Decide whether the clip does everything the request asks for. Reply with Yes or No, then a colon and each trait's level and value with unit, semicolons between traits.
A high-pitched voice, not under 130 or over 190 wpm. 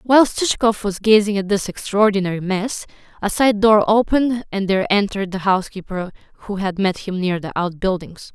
Yes: high, 200 Hz; average, 175 wpm